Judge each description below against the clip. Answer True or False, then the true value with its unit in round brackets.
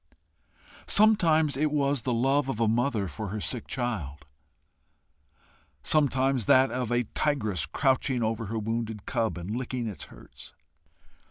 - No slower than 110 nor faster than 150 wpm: True (140 wpm)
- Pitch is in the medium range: False (120 Hz)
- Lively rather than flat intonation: False (3.9 semitones)